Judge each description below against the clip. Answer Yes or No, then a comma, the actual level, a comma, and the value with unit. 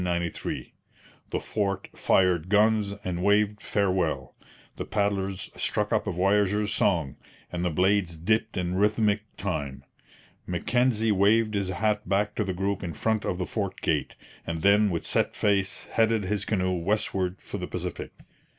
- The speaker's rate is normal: Yes, average, 150 wpm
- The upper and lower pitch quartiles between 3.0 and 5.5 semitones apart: No, narrow, 2.6 semitones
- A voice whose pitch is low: Yes, low, 100 Hz